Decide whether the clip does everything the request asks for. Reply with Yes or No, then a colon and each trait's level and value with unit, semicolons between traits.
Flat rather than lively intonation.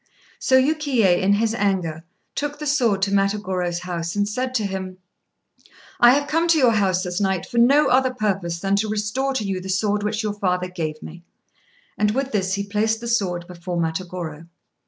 No: average, 4.5 semitones